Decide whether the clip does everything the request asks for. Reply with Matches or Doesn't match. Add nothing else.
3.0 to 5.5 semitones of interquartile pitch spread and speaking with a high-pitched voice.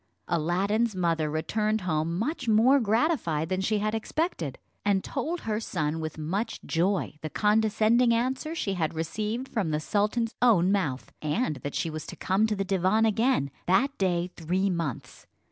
Matches